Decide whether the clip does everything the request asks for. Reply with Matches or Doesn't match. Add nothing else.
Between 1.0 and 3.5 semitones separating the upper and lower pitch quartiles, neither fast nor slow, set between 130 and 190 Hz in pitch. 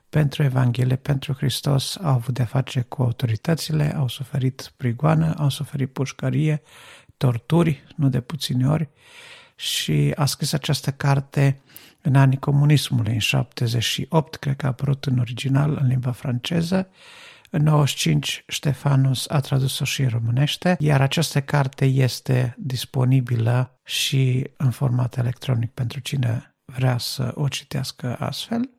Matches